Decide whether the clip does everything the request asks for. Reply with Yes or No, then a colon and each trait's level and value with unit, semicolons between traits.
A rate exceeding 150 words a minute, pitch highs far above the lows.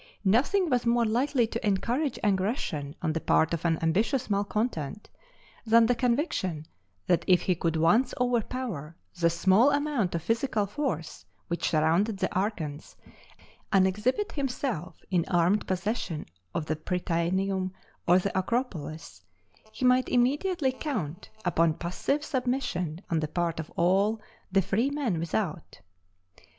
No: slow, 135 wpm; wide, 6.5 semitones